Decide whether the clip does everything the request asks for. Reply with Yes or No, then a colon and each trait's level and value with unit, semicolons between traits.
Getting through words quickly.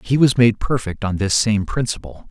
Yes: fast, 210 wpm